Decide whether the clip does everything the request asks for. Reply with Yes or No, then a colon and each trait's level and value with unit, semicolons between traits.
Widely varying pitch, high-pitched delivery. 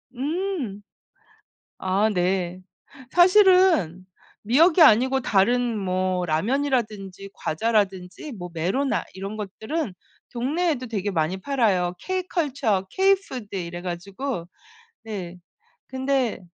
Yes: wide, 6.9 semitones; high, 215 Hz